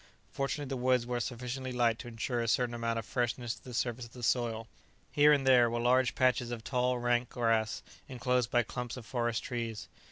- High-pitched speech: No, low, 120 Hz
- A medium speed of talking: No, fast, 210 wpm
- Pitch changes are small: Yes, narrow, 1.4 semitones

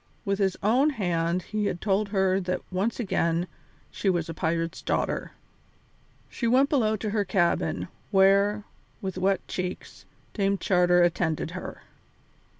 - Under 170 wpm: Yes, average, 145 wpm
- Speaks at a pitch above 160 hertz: Yes, high, 190 Hz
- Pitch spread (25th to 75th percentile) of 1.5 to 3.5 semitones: Yes, average, 2.9 semitones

